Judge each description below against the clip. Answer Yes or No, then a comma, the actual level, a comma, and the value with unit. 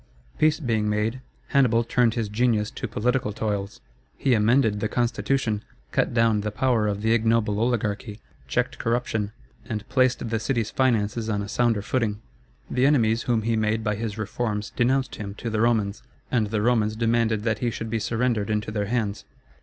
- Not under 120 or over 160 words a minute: No, average, 175 wpm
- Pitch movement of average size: No, narrow, 2.2 semitones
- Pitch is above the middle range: No, low, 110 Hz